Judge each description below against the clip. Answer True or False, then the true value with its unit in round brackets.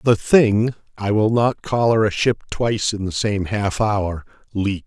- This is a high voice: False (105 Hz)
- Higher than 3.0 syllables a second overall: False (2.9 syllables/s)